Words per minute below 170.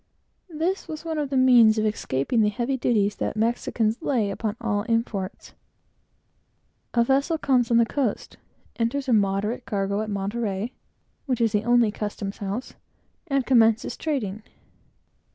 Yes: average, 150 wpm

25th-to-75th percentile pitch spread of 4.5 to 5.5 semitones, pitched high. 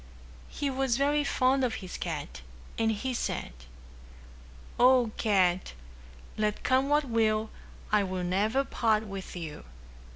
Yes: average, 5.2 semitones; high, 220 Hz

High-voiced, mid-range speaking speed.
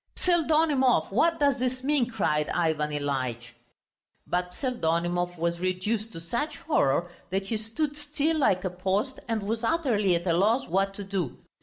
Yes: high, 200 Hz; average, 160 wpm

